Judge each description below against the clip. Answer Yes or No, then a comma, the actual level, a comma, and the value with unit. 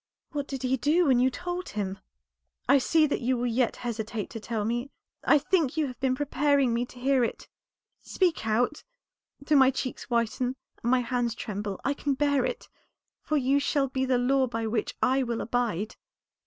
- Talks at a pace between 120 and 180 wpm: No, average, 195 wpm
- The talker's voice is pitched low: No, very high, 255 Hz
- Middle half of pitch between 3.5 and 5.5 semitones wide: No, average, 3.0 semitones